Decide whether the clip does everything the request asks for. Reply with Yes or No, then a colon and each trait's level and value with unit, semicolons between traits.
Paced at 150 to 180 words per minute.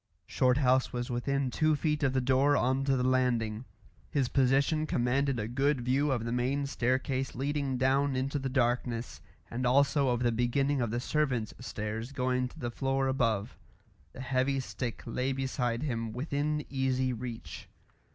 Yes: average, 165 wpm